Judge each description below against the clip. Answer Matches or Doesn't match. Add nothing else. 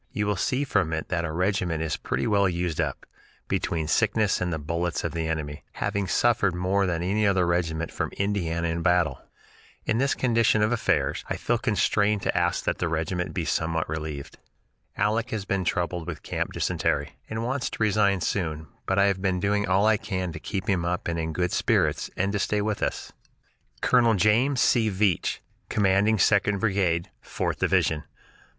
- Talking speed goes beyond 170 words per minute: Matches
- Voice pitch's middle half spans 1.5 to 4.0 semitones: Matches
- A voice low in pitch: Matches